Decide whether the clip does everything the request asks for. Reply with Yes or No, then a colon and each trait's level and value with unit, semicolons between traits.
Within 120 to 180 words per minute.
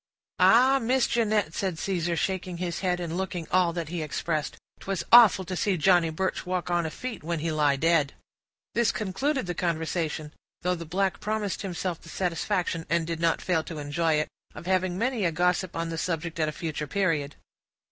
No: average, 195 wpm